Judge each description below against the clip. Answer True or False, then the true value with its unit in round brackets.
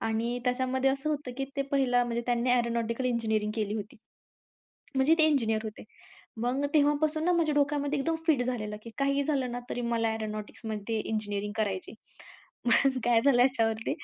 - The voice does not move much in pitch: False (3.8 semitones)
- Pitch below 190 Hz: False (245 Hz)